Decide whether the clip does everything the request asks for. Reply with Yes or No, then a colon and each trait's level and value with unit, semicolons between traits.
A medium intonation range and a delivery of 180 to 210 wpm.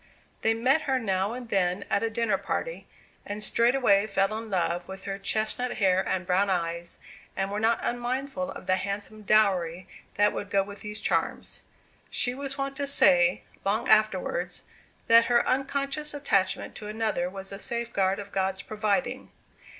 No: average, 3.8 semitones; average, 165 wpm